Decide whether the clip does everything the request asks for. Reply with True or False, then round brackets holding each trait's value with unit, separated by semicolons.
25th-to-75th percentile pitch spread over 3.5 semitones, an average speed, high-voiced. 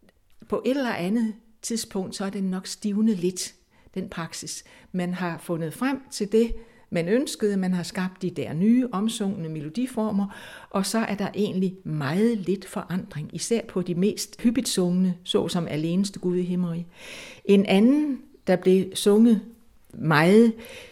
True (3.9 semitones; 155 wpm; 200 Hz)